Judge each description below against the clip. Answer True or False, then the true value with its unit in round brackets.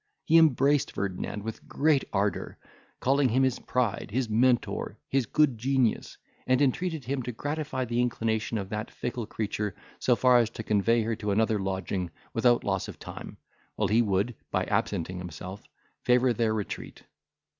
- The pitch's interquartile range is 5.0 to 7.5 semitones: False (3.8 semitones)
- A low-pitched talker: True (115 Hz)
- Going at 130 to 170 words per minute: True (165 wpm)